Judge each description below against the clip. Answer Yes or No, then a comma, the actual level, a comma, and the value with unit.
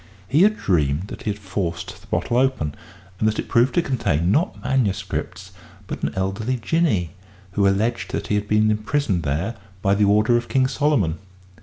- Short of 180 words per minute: No, average, 185 wpm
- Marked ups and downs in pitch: No, average, 4.6 semitones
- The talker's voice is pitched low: Yes, low, 105 Hz